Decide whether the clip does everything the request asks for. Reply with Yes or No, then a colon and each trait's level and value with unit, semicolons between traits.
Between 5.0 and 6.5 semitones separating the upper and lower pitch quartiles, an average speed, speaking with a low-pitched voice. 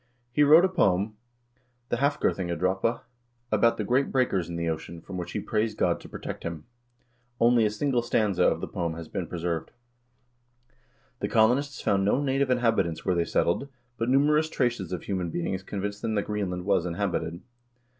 Yes: wide, 5.4 semitones; average, 175 wpm; low, 105 Hz